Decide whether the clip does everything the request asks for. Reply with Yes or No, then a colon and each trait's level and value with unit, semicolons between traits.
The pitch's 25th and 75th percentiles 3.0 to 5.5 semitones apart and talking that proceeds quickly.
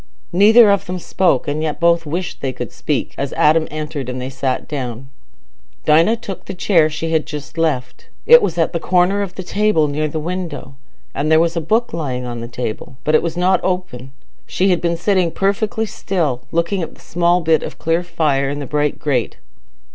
Yes: average, 4.0 semitones; fast, 210 wpm